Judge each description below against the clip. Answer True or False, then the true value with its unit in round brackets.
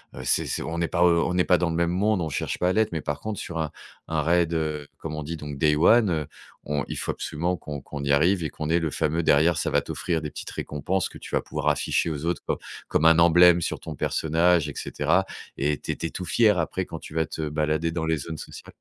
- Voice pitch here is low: True (80 Hz)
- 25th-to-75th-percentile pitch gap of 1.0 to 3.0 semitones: True (2.5 semitones)